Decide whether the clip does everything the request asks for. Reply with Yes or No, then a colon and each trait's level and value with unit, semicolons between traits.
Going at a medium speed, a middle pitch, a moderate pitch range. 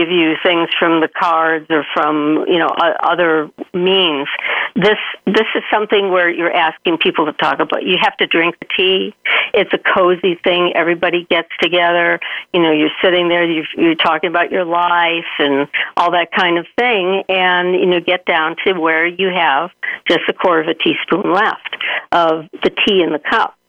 No: average, 190 wpm; medium, 175 Hz; narrow, 2.2 semitones